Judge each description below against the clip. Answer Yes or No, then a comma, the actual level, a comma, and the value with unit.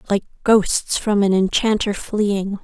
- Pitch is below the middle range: No, high, 205 Hz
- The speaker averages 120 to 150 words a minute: Yes, slow, 135 wpm